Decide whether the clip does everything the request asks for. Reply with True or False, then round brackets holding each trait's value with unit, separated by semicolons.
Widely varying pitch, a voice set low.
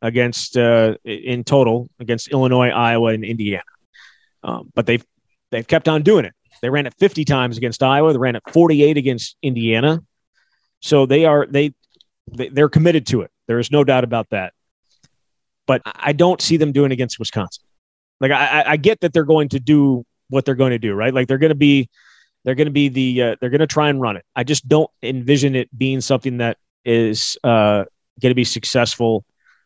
False (3.7 semitones; 130 Hz)